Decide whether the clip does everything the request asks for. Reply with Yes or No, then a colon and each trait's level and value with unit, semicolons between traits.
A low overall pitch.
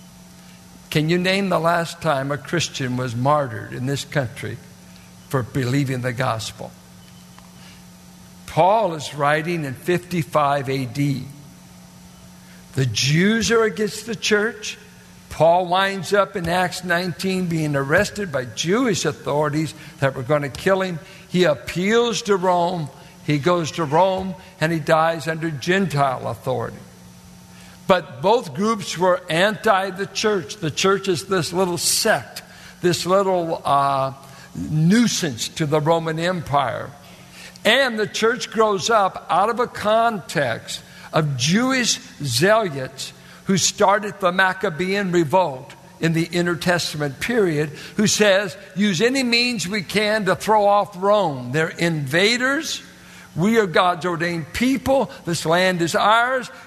No: medium, 170 Hz